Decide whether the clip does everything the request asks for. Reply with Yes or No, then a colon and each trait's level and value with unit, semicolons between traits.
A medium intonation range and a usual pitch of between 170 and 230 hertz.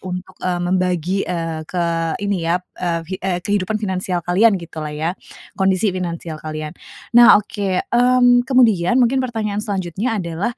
Yes: average, 3.5 semitones; medium, 185 Hz